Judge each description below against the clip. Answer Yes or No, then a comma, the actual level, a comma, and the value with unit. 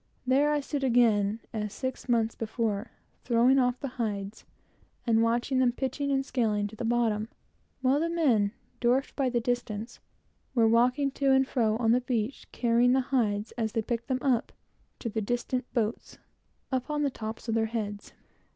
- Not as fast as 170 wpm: No, average, 175 wpm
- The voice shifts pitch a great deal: No, average, 2.8 semitones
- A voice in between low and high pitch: No, high, 240 Hz